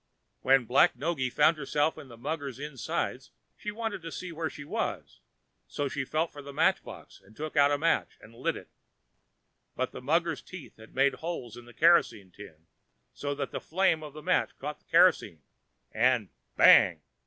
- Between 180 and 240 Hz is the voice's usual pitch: No, medium, 145 Hz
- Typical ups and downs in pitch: Yes, average, 4.3 semitones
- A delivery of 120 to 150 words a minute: No, average, 190 wpm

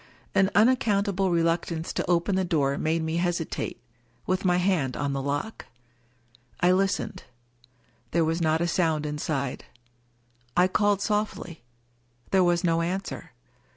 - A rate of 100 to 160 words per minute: Yes, average, 140 wpm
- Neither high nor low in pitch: Yes, medium, 175 Hz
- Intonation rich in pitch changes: No, average, 3.0 semitones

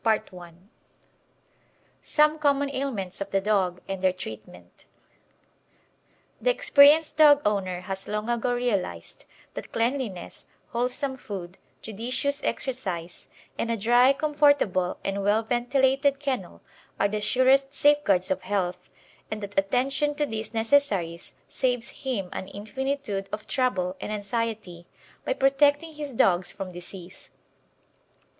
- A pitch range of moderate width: No, wide, 6.0 semitones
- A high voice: Yes, high, 225 Hz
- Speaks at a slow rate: Yes, slow, 125 wpm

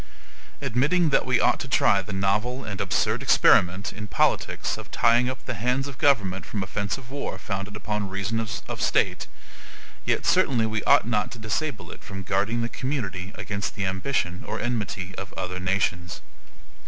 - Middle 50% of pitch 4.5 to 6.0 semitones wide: No, average, 4.0 semitones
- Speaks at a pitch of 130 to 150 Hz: No, low, 105 Hz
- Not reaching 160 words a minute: No, average, 170 wpm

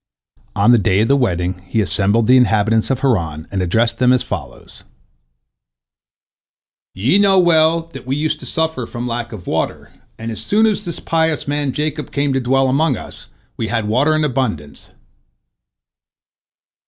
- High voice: No, low, 125 Hz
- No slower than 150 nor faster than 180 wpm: Yes, average, 165 wpm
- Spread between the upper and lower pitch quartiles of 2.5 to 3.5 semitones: No, wide, 5.6 semitones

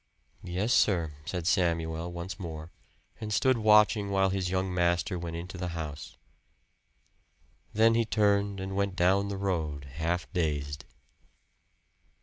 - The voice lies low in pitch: Yes, very low, 90 Hz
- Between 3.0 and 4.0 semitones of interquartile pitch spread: Yes, average, 3.3 semitones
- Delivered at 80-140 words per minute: Yes, slow, 135 wpm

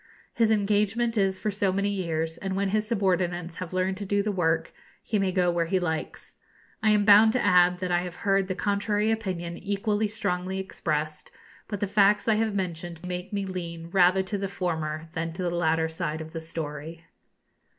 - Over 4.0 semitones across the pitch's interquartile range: No, average, 3.2 semitones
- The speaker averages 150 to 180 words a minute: No, average, 200 wpm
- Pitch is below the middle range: No, medium, 185 Hz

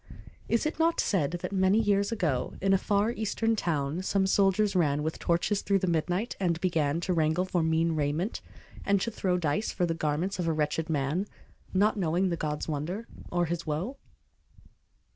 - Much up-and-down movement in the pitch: No, average, 4.0 semitones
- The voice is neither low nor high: Yes, medium, 180 Hz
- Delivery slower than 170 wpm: No, average, 185 wpm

